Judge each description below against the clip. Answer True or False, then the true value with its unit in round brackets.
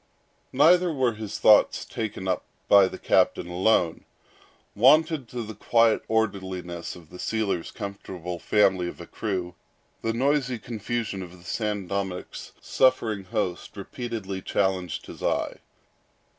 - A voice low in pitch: True (100 Hz)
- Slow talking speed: True (130 wpm)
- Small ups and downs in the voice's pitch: False (3.8 semitones)